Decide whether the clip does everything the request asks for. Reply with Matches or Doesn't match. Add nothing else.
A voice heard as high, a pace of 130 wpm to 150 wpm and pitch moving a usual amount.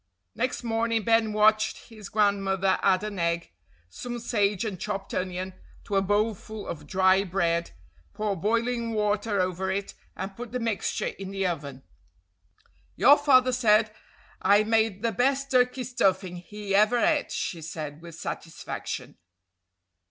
Matches